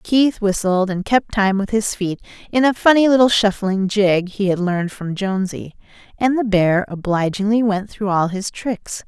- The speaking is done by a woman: Yes, female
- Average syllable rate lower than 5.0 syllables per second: Yes, 4.7 syllables/s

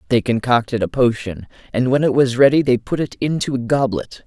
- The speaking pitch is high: No, low, 125 Hz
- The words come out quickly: Yes, fast, 210 wpm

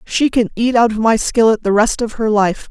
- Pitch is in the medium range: No, high, 225 Hz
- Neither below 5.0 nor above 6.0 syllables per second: Yes, 5.1 syllables/s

